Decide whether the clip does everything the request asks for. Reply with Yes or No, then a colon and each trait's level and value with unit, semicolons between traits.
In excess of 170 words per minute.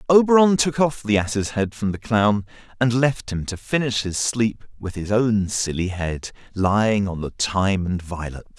Yes: average, 190 wpm